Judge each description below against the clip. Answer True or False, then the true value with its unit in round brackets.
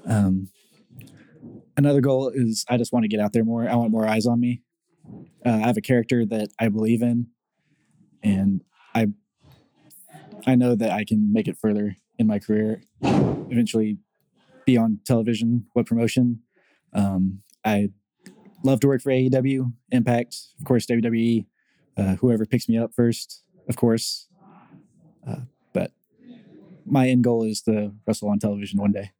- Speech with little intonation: False (3.1 semitones)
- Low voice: True (115 Hz)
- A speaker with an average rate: True (160 wpm)